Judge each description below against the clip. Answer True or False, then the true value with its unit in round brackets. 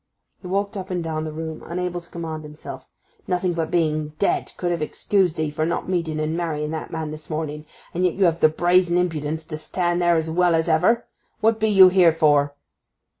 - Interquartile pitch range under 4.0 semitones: True (2.5 semitones)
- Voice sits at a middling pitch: True (165 Hz)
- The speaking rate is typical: False (215 wpm)